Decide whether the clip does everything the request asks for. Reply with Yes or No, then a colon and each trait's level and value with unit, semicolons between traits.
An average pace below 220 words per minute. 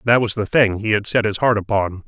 No: fast, 290 wpm